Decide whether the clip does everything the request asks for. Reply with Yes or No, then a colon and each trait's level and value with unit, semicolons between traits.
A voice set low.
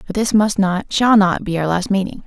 No: high, 195 Hz